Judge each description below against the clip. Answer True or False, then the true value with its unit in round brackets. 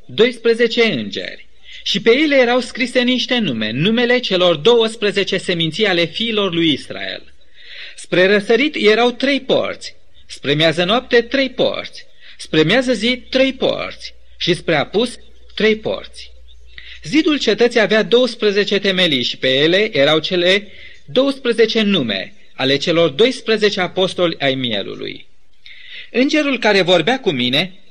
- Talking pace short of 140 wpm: True (130 wpm)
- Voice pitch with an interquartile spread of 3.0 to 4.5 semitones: False (5.4 semitones)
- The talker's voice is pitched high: True (215 Hz)